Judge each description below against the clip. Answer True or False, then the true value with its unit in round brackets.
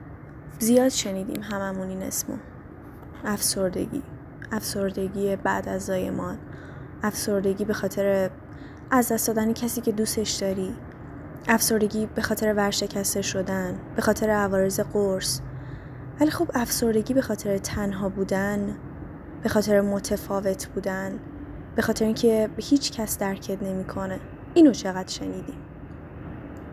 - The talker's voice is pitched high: True (200 Hz)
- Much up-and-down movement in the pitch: False (2.3 semitones)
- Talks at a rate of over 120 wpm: False (110 wpm)